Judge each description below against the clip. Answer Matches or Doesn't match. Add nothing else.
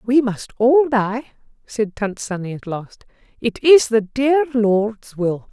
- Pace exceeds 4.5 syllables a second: Doesn't match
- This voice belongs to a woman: Matches